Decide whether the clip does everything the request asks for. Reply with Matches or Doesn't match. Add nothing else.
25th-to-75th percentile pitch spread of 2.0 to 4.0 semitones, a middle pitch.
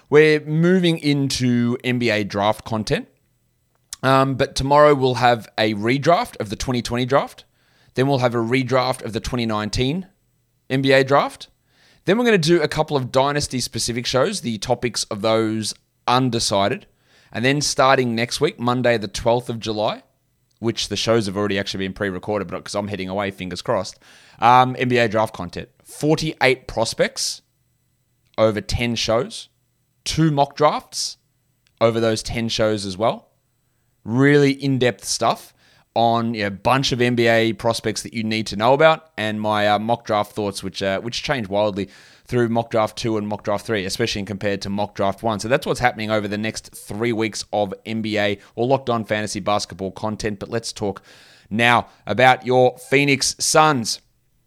Doesn't match